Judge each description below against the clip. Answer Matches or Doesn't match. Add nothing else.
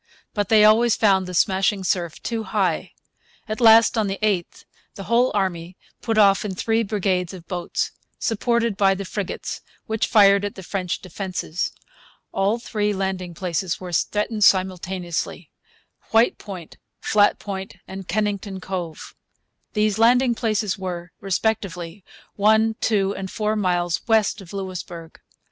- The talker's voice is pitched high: Matches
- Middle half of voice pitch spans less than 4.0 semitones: Matches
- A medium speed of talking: Matches